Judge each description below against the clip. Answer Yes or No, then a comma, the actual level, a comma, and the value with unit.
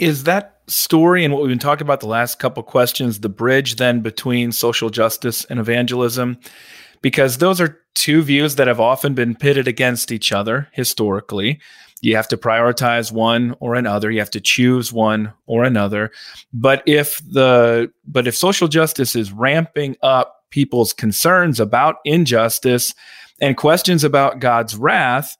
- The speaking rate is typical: Yes, average, 165 wpm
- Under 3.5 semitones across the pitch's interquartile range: No, average, 3.8 semitones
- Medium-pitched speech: No, low, 125 Hz